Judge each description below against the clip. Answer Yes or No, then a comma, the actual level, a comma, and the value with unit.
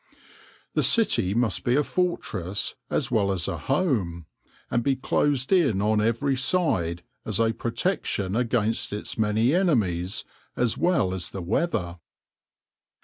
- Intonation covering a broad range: Yes, wide, 6.3 semitones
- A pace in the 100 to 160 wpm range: Yes, average, 140 wpm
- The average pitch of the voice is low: Yes, low, 115 Hz